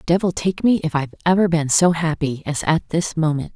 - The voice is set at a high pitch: No, medium, 165 Hz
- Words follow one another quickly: Yes, fast, 220 wpm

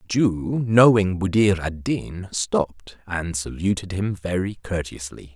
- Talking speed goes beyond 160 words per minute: No, slow, 135 wpm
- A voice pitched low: Yes, very low, 95 Hz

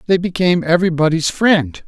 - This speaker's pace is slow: Yes, slow, 130 wpm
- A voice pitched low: No, medium, 170 Hz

